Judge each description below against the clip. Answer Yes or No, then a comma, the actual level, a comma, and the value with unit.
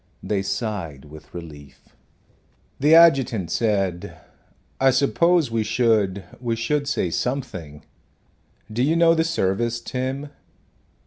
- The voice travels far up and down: Yes, wide, 6.8 semitones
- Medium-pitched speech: No, low, 115 Hz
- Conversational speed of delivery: No, slow, 115 wpm